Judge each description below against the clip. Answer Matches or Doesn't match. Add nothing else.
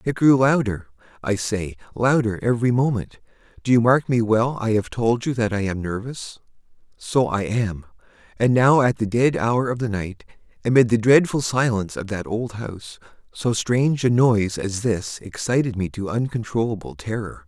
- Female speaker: Doesn't match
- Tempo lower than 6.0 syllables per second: Matches